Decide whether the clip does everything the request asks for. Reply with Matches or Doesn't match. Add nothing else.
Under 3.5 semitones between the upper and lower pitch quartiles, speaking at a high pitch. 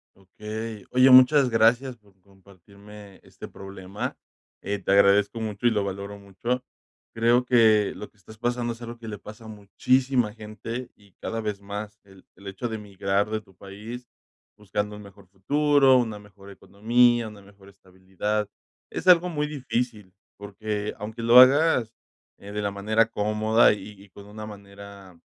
Doesn't match